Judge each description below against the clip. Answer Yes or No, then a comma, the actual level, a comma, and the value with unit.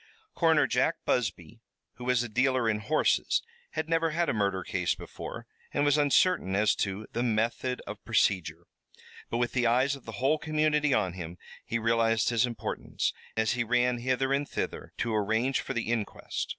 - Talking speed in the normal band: Yes, average, 180 wpm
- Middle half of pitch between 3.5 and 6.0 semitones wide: Yes, average, 3.9 semitones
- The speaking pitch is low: Yes, low, 120 Hz